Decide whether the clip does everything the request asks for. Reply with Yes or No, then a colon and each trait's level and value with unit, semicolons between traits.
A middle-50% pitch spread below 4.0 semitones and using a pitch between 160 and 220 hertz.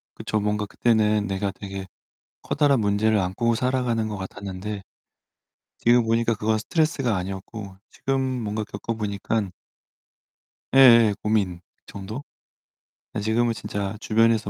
No: narrow, 2.4 semitones; low, 110 Hz